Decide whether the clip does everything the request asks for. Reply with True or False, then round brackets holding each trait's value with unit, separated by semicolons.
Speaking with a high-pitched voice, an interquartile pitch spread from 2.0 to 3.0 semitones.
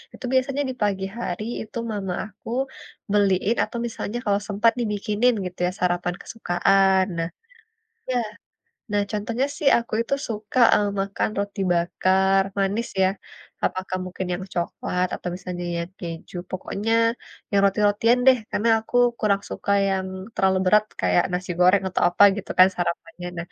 True (195 Hz; 2.7 semitones)